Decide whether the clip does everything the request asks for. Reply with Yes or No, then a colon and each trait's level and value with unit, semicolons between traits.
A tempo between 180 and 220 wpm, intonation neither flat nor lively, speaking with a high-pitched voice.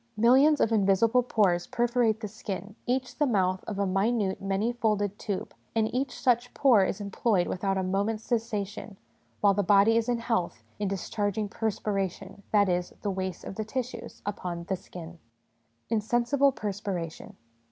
No: average, 160 wpm; average, 3.2 semitones; high, 205 Hz